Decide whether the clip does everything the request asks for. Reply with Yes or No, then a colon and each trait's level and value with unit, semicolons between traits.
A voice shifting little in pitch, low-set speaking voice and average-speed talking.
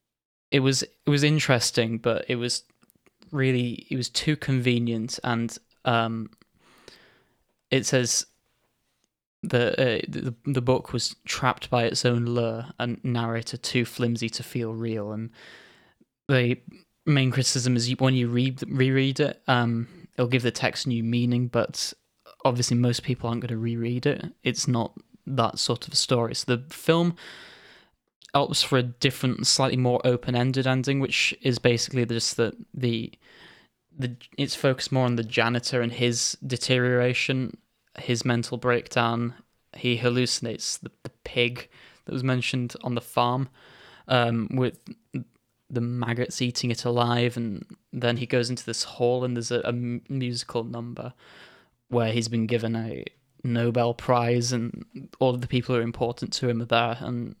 Yes: narrow, 1.6 semitones; low, 120 Hz; average, 155 wpm